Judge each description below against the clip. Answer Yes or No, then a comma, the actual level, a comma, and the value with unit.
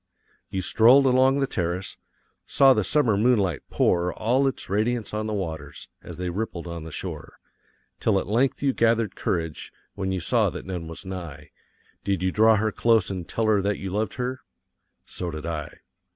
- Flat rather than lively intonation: No, average, 4.5 semitones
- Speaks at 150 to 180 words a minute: No, average, 190 wpm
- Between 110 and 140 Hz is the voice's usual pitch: No, low, 100 Hz